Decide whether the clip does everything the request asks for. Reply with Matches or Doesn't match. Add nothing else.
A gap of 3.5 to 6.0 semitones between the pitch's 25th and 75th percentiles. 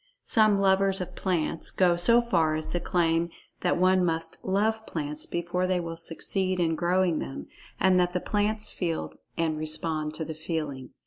Doesn't match